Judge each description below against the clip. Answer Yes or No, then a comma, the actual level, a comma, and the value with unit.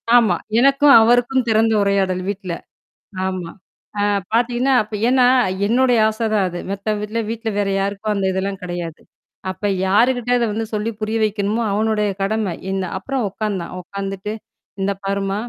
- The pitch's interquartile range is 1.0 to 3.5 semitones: Yes, average, 2.8 semitones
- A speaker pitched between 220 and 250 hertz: No, high, 210 Hz